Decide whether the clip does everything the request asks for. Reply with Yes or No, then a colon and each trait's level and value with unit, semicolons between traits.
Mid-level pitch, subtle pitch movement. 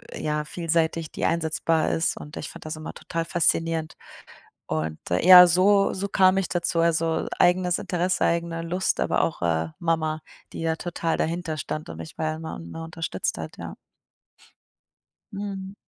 Yes: medium, 165 Hz; narrow, 2.1 semitones